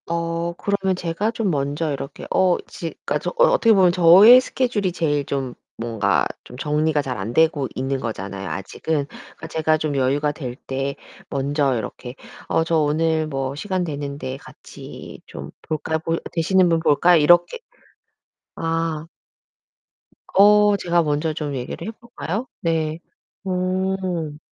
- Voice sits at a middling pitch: Yes, medium, 160 Hz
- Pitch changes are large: No, average, 4.2 semitones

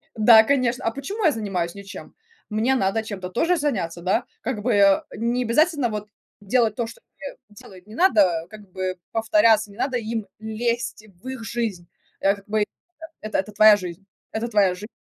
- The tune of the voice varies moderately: Yes, average, 3.2 semitones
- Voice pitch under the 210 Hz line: No, high, 220 Hz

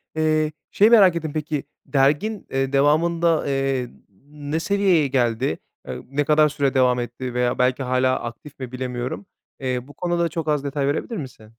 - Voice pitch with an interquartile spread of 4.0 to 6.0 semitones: No, average, 3.5 semitones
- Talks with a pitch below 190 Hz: Yes, medium, 140 Hz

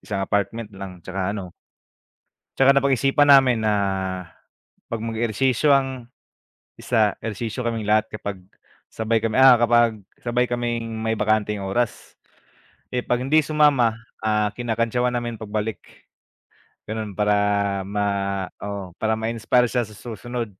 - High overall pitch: No, low, 115 Hz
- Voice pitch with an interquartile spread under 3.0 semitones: Yes, narrow, 2.6 semitones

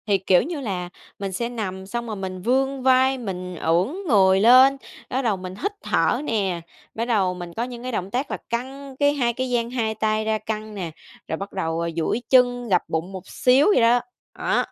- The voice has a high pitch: Yes, high, 220 Hz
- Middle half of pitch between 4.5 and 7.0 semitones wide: Yes, average, 4.9 semitones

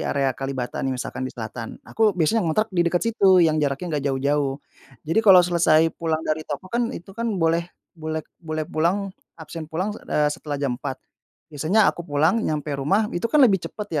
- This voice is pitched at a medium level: Yes, medium, 160 Hz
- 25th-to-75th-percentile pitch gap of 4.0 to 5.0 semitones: Yes, average, 4.4 semitones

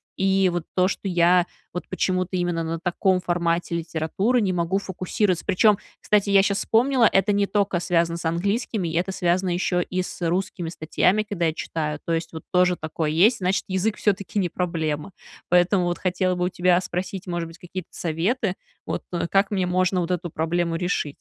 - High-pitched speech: No, medium, 180 Hz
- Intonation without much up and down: Yes, narrow, 2.3 semitones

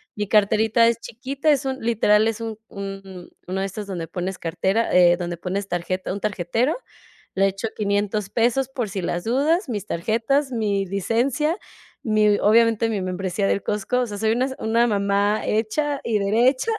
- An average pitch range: Yes, average, 3.1 semitones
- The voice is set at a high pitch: Yes, high, 210 Hz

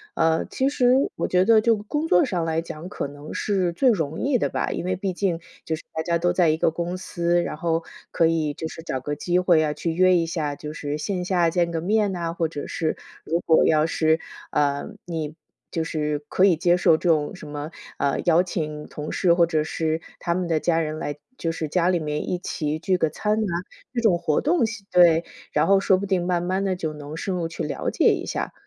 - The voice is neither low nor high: Yes, medium, 170 Hz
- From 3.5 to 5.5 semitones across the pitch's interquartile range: No, average, 2.7 semitones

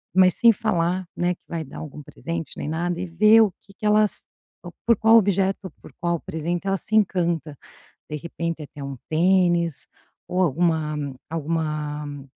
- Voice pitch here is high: No, medium, 170 Hz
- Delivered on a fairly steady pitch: No, average, 3.2 semitones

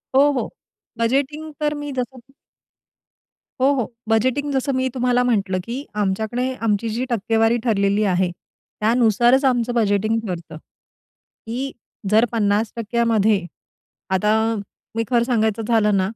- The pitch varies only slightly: No, average, 3.1 semitones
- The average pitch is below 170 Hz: No, high, 230 Hz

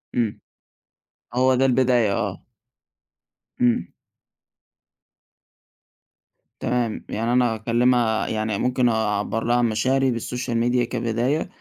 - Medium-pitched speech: No, low, 120 Hz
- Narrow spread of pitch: Yes, narrow, 2.0 semitones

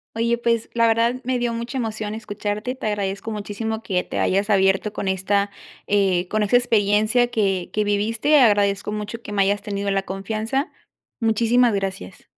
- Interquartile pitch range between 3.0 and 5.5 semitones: No, narrow, 2.5 semitones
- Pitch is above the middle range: Yes, high, 210 Hz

